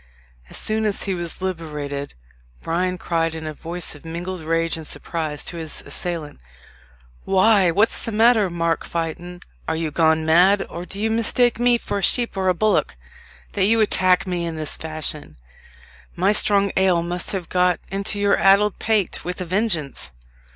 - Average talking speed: Yes, average, 175 wpm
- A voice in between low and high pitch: Yes, medium, 180 Hz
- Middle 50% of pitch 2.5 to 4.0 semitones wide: Yes, average, 3.5 semitones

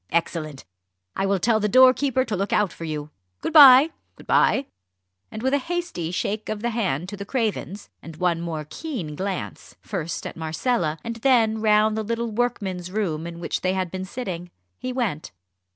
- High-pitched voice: Yes, high, 205 Hz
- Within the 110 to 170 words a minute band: No, average, 185 wpm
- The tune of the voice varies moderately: No, wide, 5.8 semitones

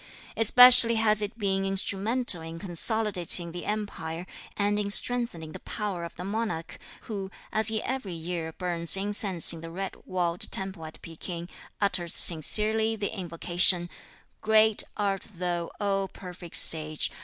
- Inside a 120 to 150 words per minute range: Yes, average, 145 wpm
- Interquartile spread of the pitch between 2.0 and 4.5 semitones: Yes, average, 3.7 semitones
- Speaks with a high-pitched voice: Yes, high, 195 Hz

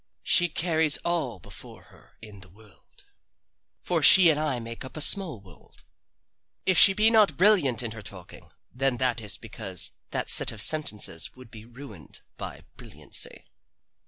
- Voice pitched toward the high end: No, low, 125 Hz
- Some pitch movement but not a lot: No, wide, 7.0 semitones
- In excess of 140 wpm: Yes, average, 160 wpm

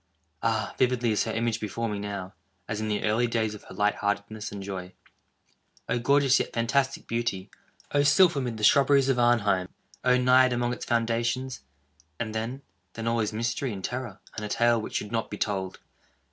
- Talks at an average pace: Yes, average, 190 wpm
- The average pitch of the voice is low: Yes, low, 115 Hz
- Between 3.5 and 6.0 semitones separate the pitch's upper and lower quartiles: No, average, 3.1 semitones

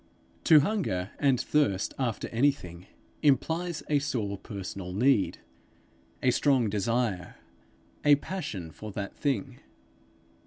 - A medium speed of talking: No, slow, 110 wpm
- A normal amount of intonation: No, wide, 6.6 semitones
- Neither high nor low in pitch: No, low, 120 Hz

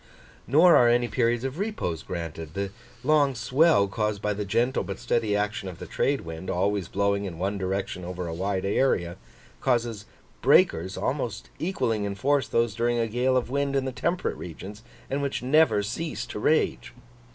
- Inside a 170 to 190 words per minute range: Yes, average, 180 wpm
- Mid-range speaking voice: No, low, 115 Hz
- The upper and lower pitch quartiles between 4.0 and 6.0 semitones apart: Yes, average, 5.1 semitones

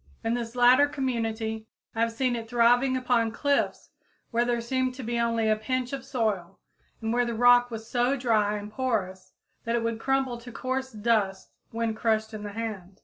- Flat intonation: Yes, narrow, 2.2 semitones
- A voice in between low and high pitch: No, high, 230 Hz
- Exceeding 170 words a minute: Yes, average, 195 wpm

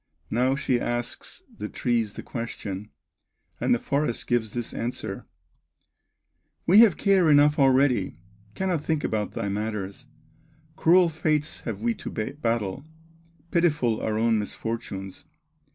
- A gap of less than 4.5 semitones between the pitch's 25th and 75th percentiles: No, wide, 5.4 semitones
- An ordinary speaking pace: No, slow, 125 wpm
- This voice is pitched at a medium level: No, low, 120 Hz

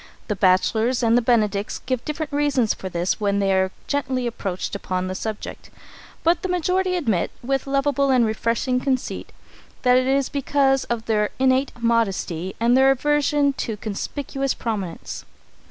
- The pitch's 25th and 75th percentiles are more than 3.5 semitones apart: Yes, average, 4.8 semitones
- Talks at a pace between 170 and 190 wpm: No, average, 155 wpm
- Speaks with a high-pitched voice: Yes, high, 245 Hz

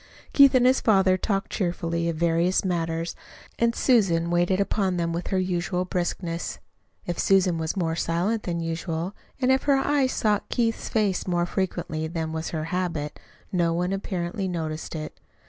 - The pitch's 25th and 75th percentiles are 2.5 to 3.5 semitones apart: Yes, average, 2.8 semitones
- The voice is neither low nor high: Yes, medium, 180 Hz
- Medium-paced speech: Yes, average, 165 wpm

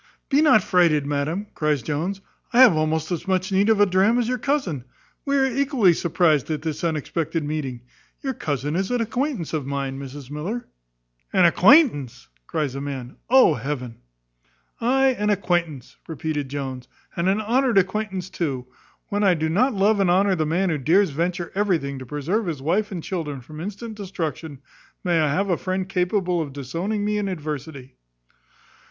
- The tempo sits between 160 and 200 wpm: Yes, average, 175 wpm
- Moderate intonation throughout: No, wide, 5.7 semitones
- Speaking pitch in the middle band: Yes, medium, 175 Hz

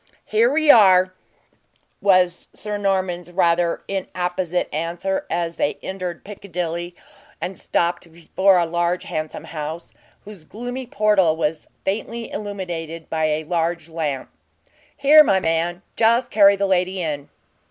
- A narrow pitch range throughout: No, average, 3.0 semitones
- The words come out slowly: Yes, slow, 130 wpm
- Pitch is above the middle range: No, medium, 180 Hz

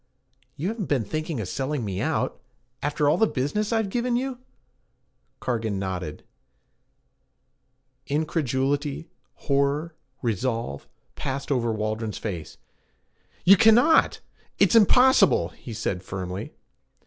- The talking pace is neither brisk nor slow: No, slow, 110 wpm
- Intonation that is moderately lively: No, wide, 8.8 semitones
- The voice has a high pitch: No, medium, 140 Hz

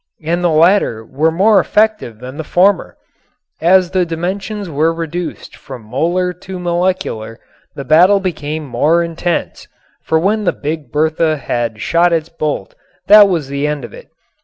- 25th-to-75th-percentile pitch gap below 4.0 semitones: Yes, average, 3.6 semitones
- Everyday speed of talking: Yes, average, 160 wpm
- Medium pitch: Yes, medium, 165 Hz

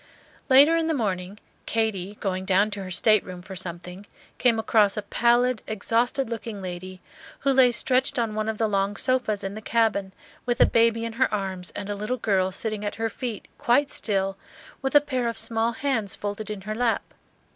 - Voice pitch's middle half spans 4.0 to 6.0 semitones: No, average, 3.4 semitones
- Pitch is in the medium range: No, high, 215 Hz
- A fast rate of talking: No, average, 195 wpm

